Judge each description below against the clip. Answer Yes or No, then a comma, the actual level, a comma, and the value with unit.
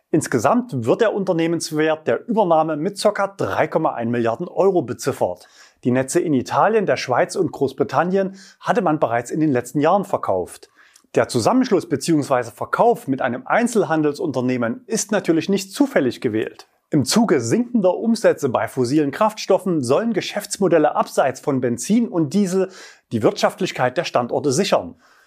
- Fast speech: No, average, 140 wpm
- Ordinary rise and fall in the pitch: No, wide, 6.3 semitones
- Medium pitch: Yes, medium, 170 Hz